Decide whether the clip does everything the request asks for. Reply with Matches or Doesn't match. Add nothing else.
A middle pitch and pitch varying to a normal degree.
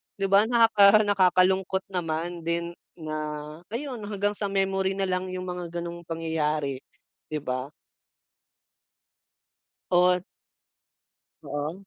Matches